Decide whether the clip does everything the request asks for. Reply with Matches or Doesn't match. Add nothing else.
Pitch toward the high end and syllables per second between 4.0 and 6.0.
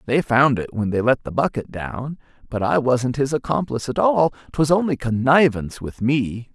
Doesn't match